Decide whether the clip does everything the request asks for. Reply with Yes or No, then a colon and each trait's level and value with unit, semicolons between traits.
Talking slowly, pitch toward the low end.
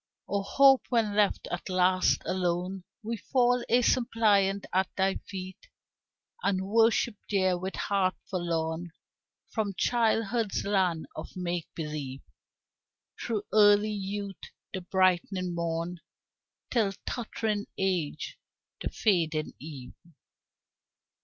No: slow, 105 wpm; high, 190 Hz